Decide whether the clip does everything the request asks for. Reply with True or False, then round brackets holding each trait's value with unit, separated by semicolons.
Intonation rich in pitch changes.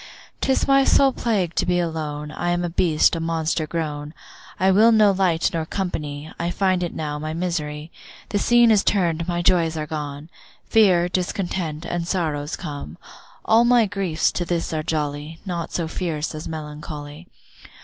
False (3.2 semitones)